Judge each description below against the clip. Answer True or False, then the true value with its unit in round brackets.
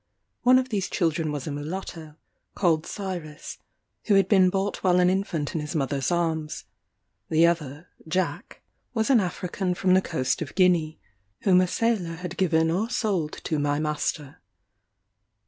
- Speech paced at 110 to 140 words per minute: False (160 wpm)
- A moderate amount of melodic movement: True (3.5 semitones)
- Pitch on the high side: False (175 Hz)